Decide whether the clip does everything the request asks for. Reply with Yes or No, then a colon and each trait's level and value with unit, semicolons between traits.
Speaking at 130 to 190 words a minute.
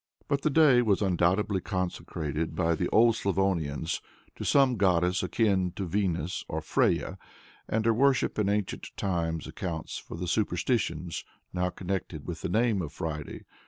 Yes: average, 155 wpm